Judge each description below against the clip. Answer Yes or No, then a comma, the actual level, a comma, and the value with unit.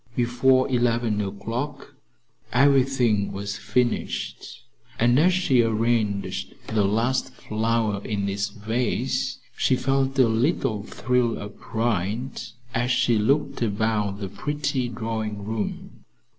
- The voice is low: Yes, low, 115 Hz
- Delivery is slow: Yes, slow, 115 wpm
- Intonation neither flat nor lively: Yes, average, 3.4 semitones